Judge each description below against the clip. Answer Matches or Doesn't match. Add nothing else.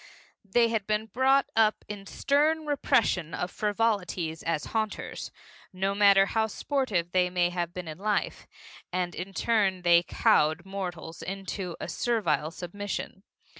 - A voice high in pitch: Matches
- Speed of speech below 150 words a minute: Matches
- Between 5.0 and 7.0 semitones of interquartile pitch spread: Doesn't match